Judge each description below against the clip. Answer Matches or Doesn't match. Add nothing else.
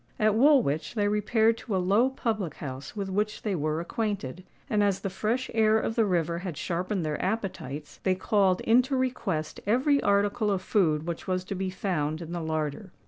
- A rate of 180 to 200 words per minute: Matches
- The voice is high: Matches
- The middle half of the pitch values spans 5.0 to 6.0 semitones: Doesn't match